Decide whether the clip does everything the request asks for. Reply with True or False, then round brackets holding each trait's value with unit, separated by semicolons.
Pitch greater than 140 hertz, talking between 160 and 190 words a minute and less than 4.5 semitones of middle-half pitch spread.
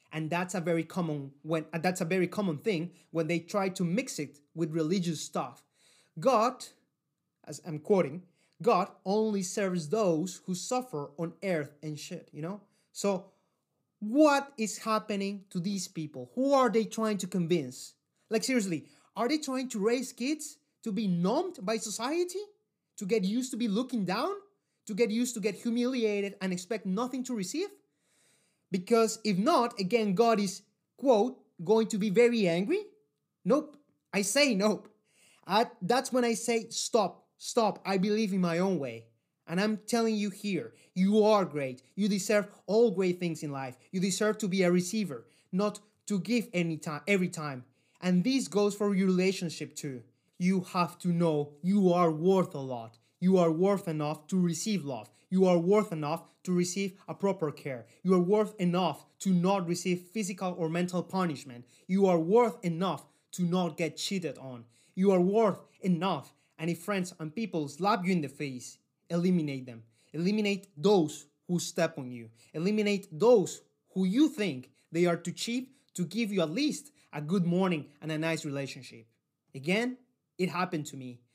False (185 Hz; 175 wpm; 4.8 semitones)